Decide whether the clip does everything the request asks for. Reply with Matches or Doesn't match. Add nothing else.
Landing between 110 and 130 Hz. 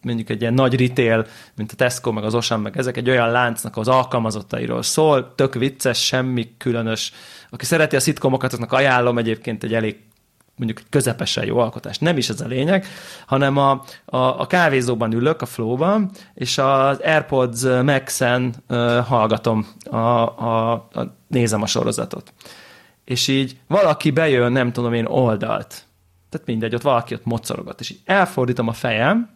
Matches